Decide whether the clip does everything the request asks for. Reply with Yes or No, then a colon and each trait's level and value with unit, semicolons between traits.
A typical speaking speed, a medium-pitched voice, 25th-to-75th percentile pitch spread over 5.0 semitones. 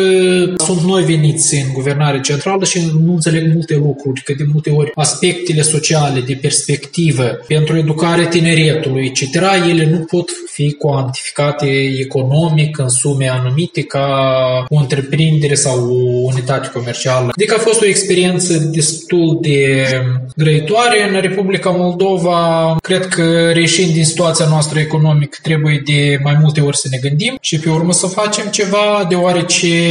No: average, 145 wpm; medium, 155 Hz; average, 3.6 semitones